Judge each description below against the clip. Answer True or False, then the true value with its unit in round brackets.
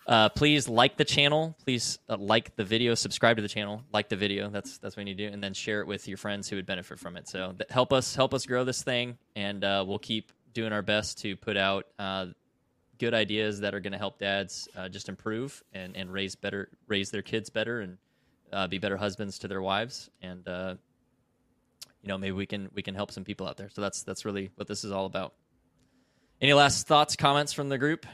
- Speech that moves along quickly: True (240 wpm)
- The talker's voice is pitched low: True (105 Hz)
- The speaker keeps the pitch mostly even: False (3.4 semitones)